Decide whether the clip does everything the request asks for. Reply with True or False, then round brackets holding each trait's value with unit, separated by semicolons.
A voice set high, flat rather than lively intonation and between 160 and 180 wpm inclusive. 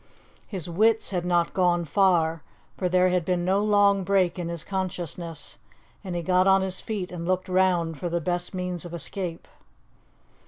False (180 Hz; 1.7 semitones; 175 wpm)